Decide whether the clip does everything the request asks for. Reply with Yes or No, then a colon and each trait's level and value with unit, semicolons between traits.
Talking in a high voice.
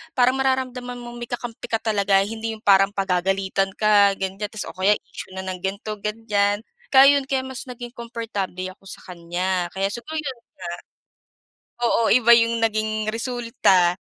Yes: high, 215 Hz